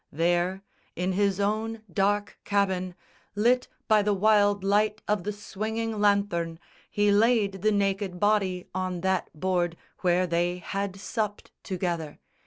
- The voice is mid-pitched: No, high, 200 Hz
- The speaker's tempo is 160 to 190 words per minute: No, slow, 135 wpm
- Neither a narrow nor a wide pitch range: No, narrow, 2.3 semitones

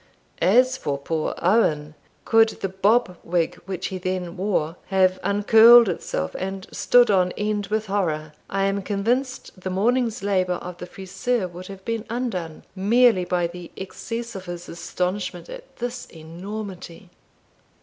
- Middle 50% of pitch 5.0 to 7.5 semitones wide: No, average, 3.8 semitones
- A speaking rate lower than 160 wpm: Yes, average, 150 wpm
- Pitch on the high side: Yes, high, 195 Hz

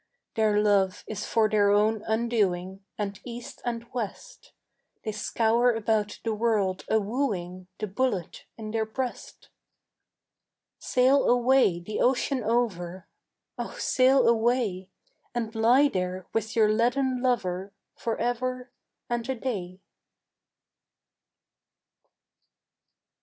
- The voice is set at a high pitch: Yes, high, 220 Hz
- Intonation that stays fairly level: No, average, 3.3 semitones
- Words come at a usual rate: No, slow, 110 wpm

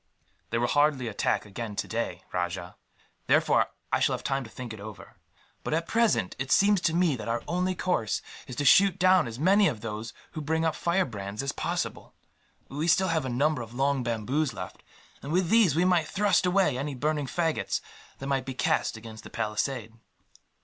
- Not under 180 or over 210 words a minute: Yes, average, 195 wpm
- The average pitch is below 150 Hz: Yes, medium, 140 Hz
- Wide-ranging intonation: Yes, wide, 6.8 semitones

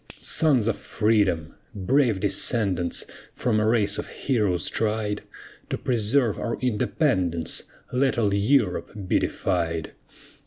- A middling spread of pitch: Yes, average, 4.1 semitones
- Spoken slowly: Yes, slow, 115 wpm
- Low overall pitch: Yes, low, 105 Hz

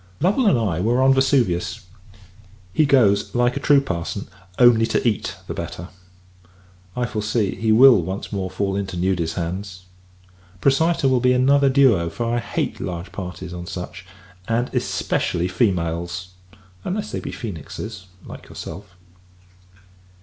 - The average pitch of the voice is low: Yes, low, 105 Hz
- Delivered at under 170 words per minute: Yes, average, 140 wpm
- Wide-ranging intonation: Yes, wide, 5.8 semitones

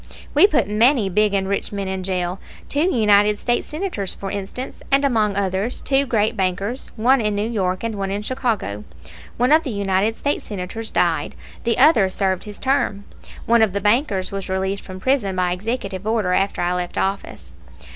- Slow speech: No, average, 185 wpm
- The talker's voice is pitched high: Yes, high, 205 Hz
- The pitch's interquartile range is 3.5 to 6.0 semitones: Yes, average, 3.8 semitones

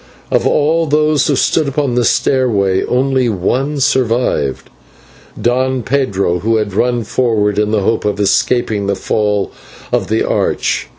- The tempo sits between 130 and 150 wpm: Yes, average, 145 wpm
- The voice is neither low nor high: No, low, 120 Hz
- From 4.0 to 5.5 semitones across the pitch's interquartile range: Yes, average, 4.4 semitones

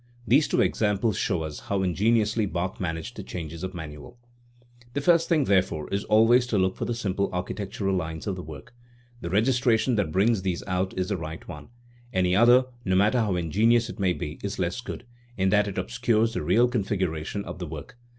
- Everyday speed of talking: No, fast, 210 wpm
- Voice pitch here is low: Yes, very low, 95 Hz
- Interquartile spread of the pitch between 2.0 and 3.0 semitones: No, average, 4.2 semitones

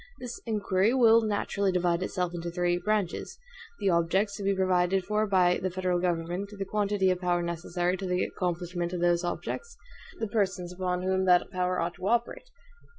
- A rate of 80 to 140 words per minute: No, average, 180 wpm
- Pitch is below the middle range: No, medium, 185 Hz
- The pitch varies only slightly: Yes, narrow, 2.2 semitones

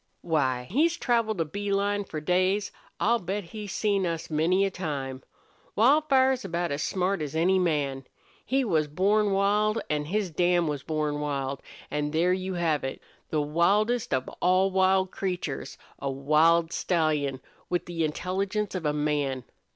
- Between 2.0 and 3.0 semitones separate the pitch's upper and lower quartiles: No, average, 4.8 semitones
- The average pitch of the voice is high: No, medium, 175 Hz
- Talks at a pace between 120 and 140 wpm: No, average, 160 wpm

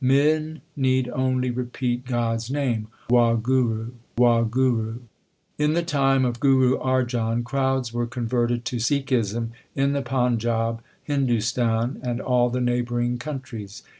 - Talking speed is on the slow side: Yes, slow, 130 wpm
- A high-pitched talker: No, low, 125 Hz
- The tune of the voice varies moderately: No, narrow, 1.9 semitones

